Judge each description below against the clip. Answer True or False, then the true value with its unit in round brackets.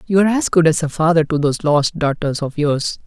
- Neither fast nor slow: False (255 wpm)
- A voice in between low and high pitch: True (160 Hz)